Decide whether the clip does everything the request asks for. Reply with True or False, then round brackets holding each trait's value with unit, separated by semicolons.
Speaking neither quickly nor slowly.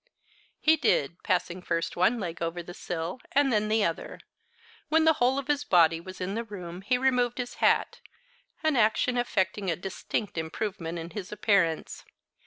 True (175 wpm)